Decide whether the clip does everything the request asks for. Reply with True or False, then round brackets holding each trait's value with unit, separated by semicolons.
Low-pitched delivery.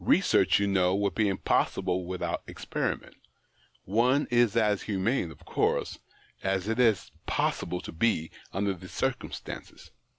True (100 Hz)